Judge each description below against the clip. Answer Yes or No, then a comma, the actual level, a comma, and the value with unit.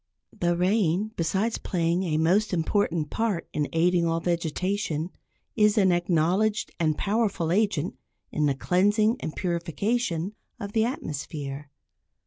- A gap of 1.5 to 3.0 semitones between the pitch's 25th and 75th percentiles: No, average, 4.1 semitones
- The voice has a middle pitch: Yes, medium, 180 Hz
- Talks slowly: Yes, slow, 125 wpm